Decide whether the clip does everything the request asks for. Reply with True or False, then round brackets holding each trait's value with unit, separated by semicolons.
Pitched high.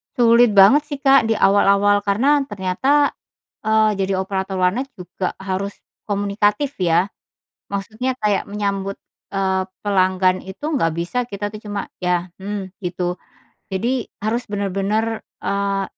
True (200 Hz)